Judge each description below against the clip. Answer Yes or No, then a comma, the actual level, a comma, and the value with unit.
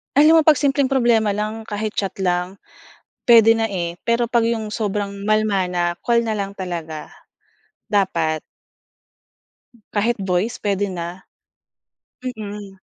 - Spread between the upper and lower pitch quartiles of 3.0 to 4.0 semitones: Yes, average, 3.4 semitones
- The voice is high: Yes, high, 210 Hz